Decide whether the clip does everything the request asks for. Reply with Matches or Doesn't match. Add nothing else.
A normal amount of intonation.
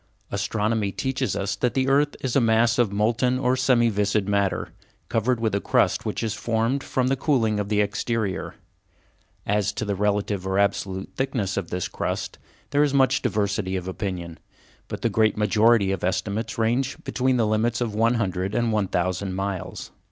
Matches